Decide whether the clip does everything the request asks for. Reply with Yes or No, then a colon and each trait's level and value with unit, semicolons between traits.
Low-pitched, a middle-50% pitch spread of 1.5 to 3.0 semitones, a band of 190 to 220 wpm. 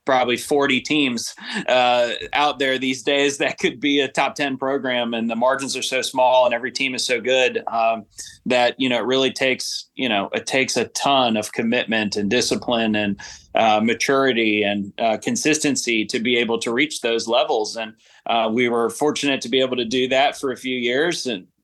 Yes: low, 125 Hz; average, 2.7 semitones; average, 200 wpm